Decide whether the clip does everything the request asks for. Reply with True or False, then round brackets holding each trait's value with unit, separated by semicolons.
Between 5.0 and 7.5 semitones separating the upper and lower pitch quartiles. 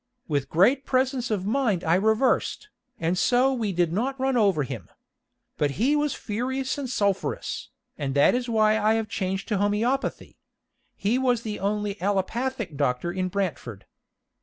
True (5.4 semitones)